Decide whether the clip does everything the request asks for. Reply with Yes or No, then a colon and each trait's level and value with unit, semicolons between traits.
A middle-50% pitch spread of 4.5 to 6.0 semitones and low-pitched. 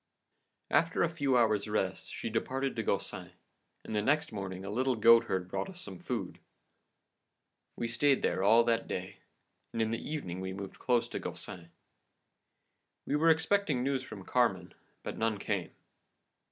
Yes: wide, 5.4 semitones; low, 115 Hz